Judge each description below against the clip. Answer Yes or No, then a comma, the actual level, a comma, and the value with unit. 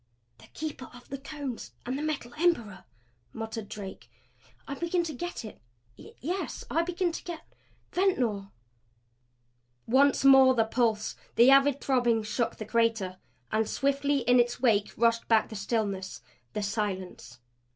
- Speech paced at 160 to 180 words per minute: No, average, 150 wpm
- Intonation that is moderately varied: Yes, average, 4.5 semitones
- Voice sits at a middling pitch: No, high, 240 Hz